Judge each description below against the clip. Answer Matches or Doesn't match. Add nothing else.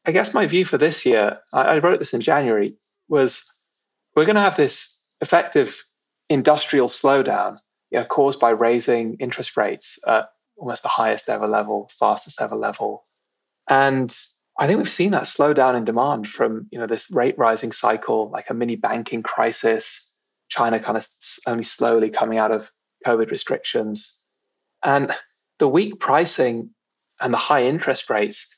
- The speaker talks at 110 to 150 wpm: Doesn't match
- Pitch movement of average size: Matches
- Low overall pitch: Matches